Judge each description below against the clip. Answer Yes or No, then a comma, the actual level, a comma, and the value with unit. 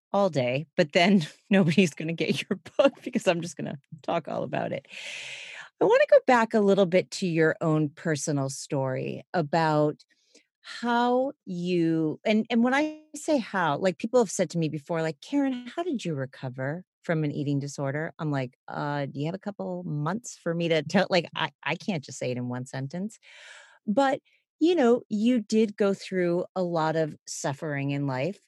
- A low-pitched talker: No, medium, 180 Hz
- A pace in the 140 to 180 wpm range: No, average, 200 wpm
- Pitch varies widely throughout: Yes, wide, 6.4 semitones